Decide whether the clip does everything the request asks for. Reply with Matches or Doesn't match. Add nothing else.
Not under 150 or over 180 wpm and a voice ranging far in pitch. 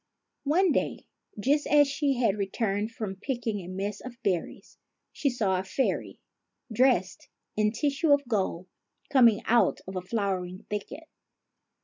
Doesn't match